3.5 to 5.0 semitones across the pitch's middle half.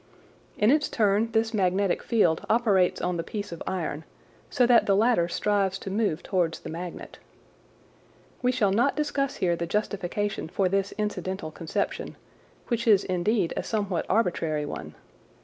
Yes: average, 3.9 semitones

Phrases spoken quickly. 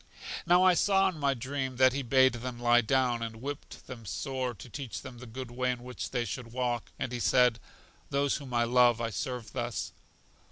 Yes: fast, 210 wpm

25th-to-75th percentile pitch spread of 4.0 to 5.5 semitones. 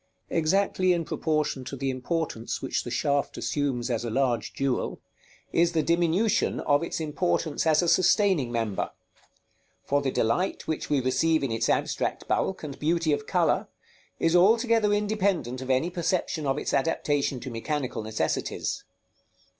Yes: average, 4.7 semitones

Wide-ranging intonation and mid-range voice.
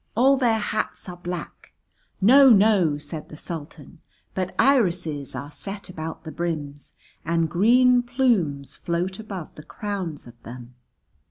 Yes: wide, 6.2 semitones; medium, 180 Hz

